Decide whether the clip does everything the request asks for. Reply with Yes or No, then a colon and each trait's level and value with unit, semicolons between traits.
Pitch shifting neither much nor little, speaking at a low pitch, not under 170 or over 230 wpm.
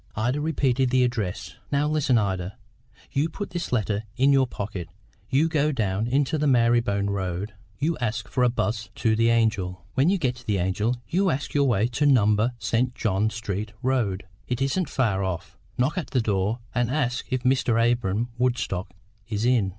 Yes: average, 4.2 semitones; low, 120 Hz; average, 185 wpm